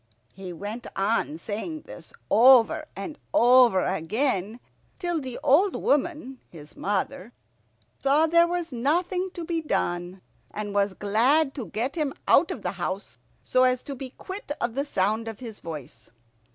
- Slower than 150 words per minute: No, average, 155 wpm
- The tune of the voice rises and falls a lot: Yes, wide, 6.9 semitones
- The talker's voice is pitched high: Yes, very high, 250 Hz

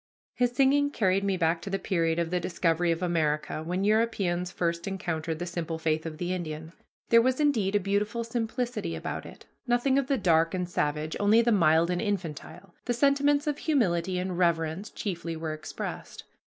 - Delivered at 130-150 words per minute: No, average, 185 wpm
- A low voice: No, medium, 180 Hz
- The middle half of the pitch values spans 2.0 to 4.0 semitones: No, wide, 5.5 semitones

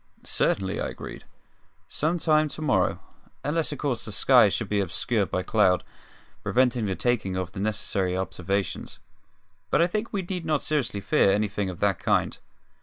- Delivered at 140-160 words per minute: No, average, 170 wpm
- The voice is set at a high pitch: No, low, 105 Hz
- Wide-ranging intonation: Yes, wide, 7.5 semitones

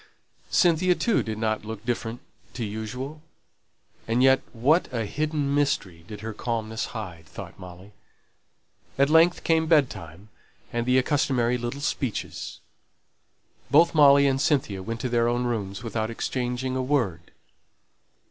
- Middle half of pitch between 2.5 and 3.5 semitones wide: No, average, 4.4 semitones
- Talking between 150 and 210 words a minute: No, average, 140 wpm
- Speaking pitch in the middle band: No, low, 120 Hz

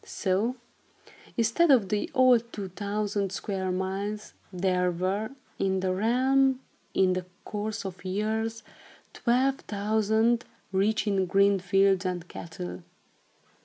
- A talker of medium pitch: No, high, 200 Hz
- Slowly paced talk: Yes, slow, 120 wpm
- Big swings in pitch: No, average, 2.9 semitones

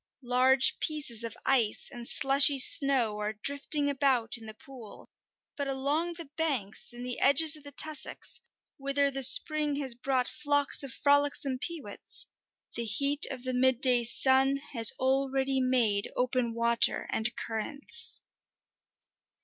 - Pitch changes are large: No, average, 3.0 semitones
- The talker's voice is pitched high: Yes, very high, 265 Hz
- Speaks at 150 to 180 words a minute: No, average, 140 wpm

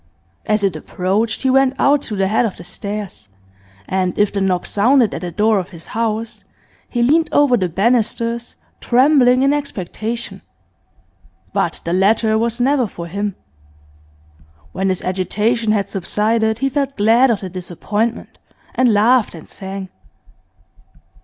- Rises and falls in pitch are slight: No, average, 4.0 semitones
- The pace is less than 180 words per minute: Yes, average, 150 wpm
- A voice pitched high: Yes, high, 215 Hz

